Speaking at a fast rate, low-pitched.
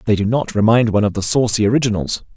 Yes: fast, 230 wpm; low, 110 Hz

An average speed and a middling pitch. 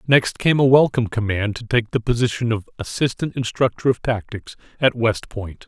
No: average, 180 wpm; low, 120 Hz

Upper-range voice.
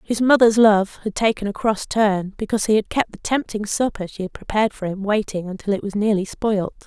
Yes: high, 210 Hz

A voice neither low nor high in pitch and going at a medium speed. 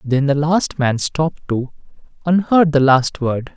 Yes: medium, 145 Hz; average, 185 wpm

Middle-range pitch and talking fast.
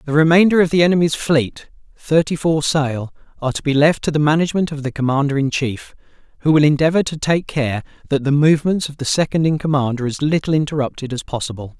Yes: medium, 150 Hz; fast, 210 wpm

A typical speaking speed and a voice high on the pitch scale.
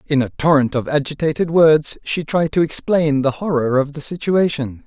No: average, 185 wpm; medium, 150 Hz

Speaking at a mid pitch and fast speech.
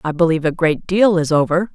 Yes: medium, 170 Hz; fast, 240 wpm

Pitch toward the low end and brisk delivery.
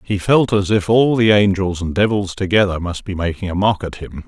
Yes: low, 100 Hz; fast, 240 wpm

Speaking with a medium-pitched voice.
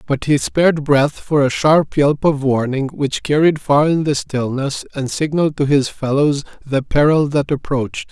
Yes: medium, 145 Hz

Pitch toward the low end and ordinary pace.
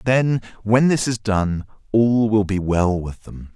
Yes: low, 105 Hz; average, 185 wpm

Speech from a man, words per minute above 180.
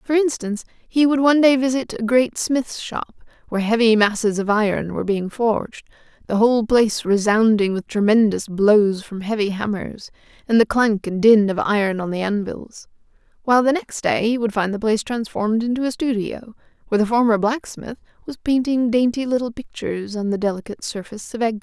No: female; average, 190 wpm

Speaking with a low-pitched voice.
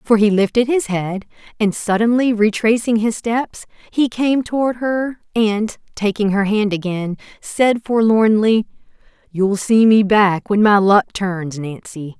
No: high, 215 Hz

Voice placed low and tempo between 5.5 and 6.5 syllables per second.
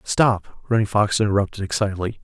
Yes: low, 105 Hz; 5.7 syllables/s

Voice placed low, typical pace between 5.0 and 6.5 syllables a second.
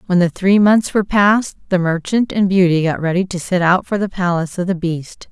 No: medium, 185 Hz; 5.4 syllables/s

